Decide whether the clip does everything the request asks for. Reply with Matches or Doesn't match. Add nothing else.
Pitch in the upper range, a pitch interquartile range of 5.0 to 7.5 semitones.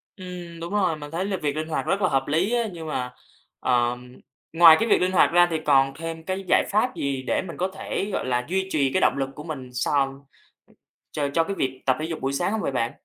Doesn't match